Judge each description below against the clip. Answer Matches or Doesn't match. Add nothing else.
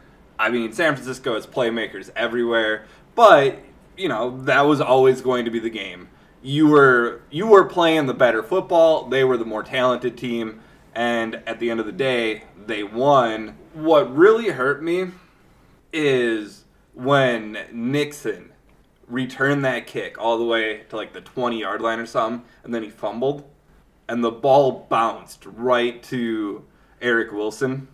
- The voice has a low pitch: Matches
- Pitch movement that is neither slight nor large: Matches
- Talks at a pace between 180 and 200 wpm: Doesn't match